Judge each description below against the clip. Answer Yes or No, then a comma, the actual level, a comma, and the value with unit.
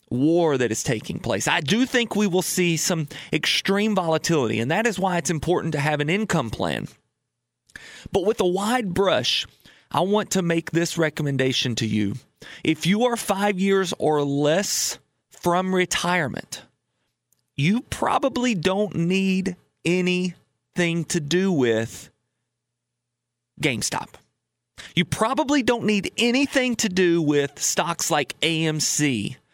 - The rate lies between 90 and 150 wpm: Yes, slow, 135 wpm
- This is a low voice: No, medium, 175 Hz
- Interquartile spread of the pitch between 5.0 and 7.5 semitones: Yes, wide, 5.4 semitones